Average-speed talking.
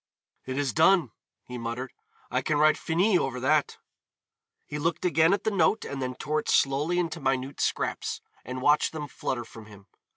Yes: average, 185 wpm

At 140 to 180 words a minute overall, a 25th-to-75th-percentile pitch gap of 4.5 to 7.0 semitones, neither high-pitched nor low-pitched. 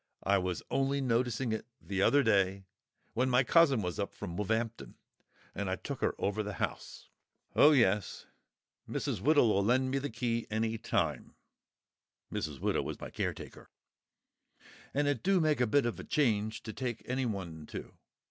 No: average, 160 wpm; average, 4.8 semitones; low, 115 Hz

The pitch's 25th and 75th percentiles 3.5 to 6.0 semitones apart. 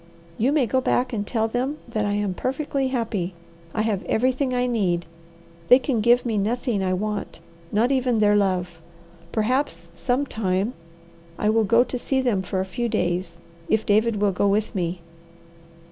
Yes: average, 3.9 semitones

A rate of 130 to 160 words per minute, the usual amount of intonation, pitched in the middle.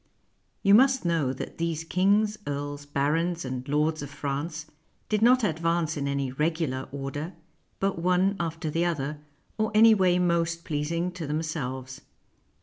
Yes: average, 150 wpm; average, 3.7 semitones; medium, 165 Hz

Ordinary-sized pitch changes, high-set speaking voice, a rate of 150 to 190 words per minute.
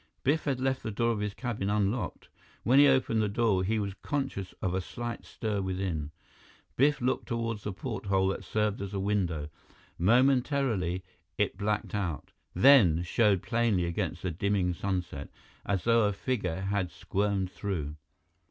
No: average, 3.8 semitones; low, 100 Hz; average, 160 wpm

